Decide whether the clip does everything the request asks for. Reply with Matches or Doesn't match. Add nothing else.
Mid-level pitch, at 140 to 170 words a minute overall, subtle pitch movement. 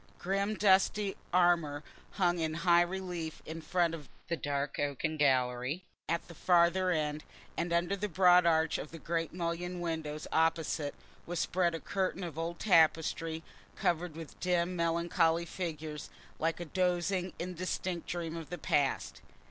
Matches